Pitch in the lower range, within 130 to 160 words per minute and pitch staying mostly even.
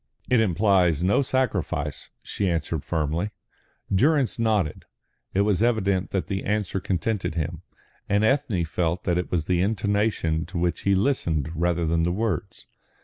No: very low, 95 Hz; average, 150 wpm; average, 4.0 semitones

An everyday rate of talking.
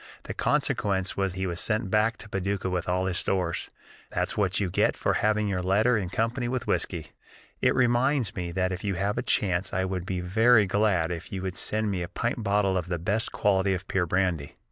No: fast, 220 wpm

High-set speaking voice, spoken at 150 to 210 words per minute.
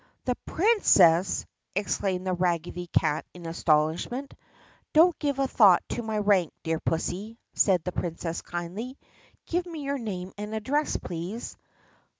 No: high, 195 Hz; average, 140 wpm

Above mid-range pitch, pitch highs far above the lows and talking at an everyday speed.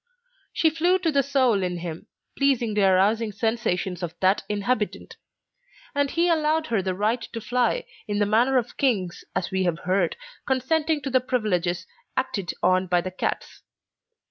Yes: high, 220 Hz; wide, 6.3 semitones; average, 160 wpm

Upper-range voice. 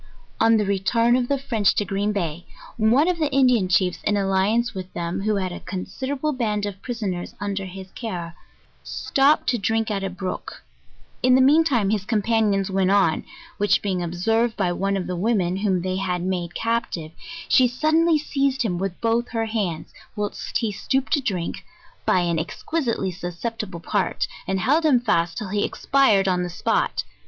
Yes: high, 205 Hz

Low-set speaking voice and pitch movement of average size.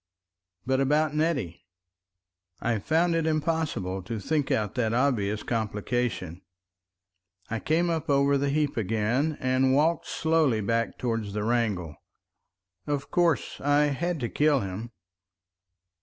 No: low, 130 Hz; wide, 5.8 semitones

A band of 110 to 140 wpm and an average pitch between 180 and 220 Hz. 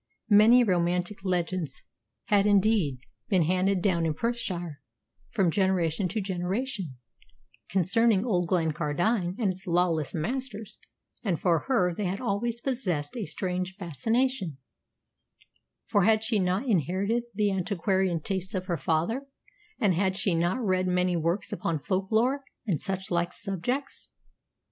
Yes: slow, 135 wpm; high, 190 Hz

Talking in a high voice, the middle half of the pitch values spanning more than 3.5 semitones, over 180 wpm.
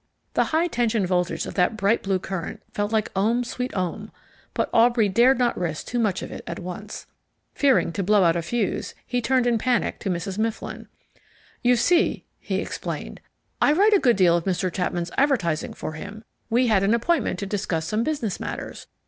Yes: high, 215 Hz; average, 4.8 semitones; average, 195 wpm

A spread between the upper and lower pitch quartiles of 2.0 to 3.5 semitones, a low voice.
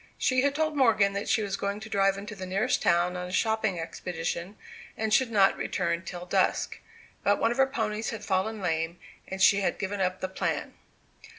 No: average, 3.1 semitones; high, 200 Hz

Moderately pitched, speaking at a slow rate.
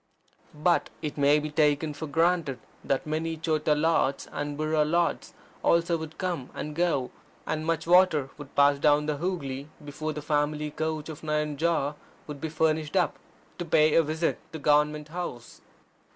No: medium, 155 Hz; average, 165 wpm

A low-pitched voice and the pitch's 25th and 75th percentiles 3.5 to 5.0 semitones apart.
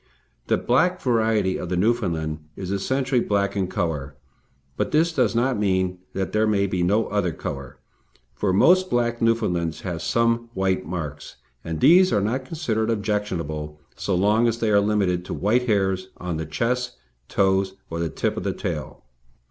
Yes: low, 100 Hz; average, 4.6 semitones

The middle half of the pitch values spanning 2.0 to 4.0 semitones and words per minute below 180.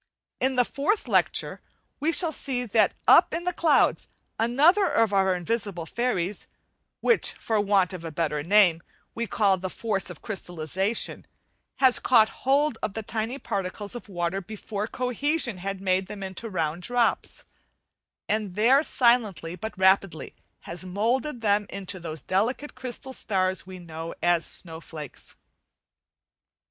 No: average, 4.8 semitones; average, 140 wpm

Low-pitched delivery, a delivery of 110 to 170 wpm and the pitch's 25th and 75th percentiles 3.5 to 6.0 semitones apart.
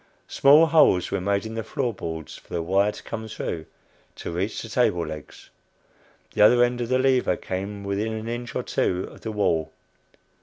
No: low, 105 Hz; average, 195 wpm; average, 4.7 semitones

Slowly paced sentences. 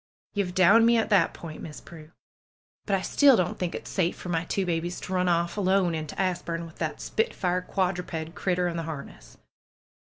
No: average, 195 wpm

